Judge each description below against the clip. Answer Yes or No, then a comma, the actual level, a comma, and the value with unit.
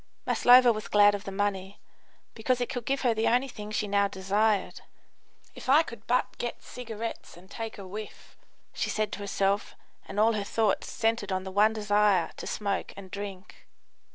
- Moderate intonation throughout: No, narrow, 2.3 semitones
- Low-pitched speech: No, high, 210 Hz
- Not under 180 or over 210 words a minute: Yes, average, 185 wpm